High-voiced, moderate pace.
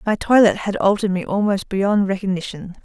Yes: high, 200 Hz; average, 170 wpm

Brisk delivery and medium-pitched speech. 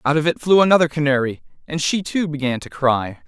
Yes: fast, 220 wpm; medium, 150 Hz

